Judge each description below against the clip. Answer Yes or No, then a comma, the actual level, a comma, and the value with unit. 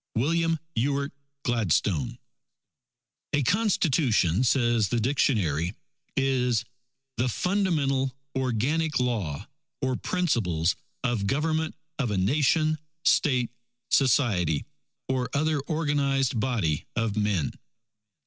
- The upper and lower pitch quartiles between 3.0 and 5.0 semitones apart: No, wide, 5.4 semitones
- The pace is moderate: No, slow, 95 wpm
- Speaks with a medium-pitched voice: No, low, 125 Hz